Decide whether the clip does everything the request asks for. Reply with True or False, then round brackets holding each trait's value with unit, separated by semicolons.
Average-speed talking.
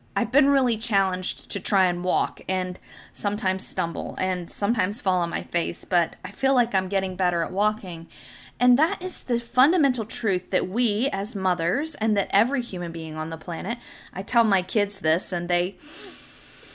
True (185 wpm)